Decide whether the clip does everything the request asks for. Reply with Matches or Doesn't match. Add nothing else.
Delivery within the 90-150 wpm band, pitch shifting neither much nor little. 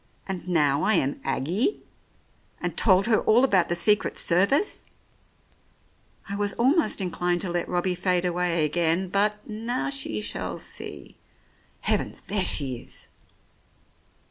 Matches